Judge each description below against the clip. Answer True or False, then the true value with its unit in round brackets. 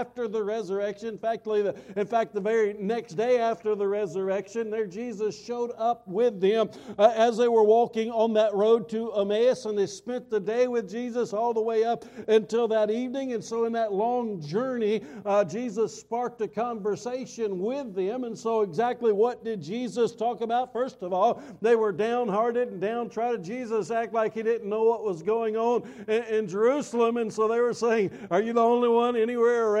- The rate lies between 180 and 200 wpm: True (195 wpm)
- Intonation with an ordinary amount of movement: False (1.8 semitones)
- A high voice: True (225 Hz)